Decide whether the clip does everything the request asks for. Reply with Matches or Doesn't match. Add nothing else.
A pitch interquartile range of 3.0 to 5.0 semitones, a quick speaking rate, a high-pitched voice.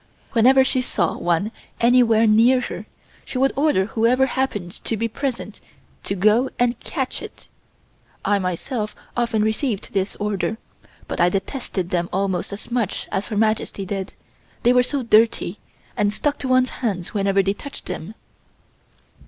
Doesn't match